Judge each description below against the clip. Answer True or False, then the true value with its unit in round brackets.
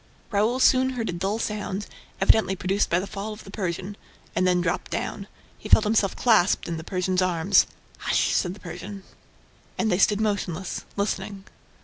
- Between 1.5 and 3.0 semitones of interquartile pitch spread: True (2.6 semitones)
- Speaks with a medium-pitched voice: False (195 Hz)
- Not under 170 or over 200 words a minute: True (175 wpm)